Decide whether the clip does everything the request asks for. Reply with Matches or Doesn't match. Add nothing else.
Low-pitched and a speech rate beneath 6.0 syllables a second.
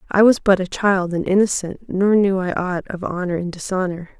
Doesn't match